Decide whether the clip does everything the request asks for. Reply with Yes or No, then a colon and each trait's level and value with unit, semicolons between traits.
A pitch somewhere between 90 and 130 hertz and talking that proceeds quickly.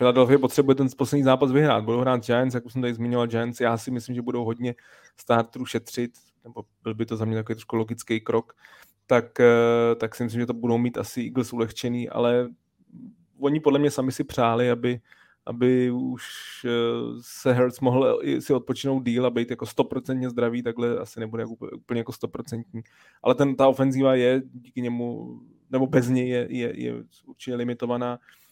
Yes: low, 120 Hz; fast, 185 wpm